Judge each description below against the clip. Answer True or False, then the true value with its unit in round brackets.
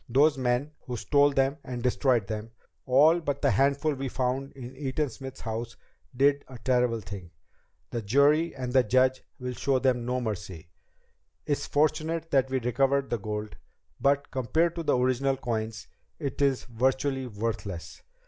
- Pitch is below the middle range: True (130 Hz)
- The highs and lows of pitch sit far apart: False (2.9 semitones)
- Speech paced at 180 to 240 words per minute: False (160 wpm)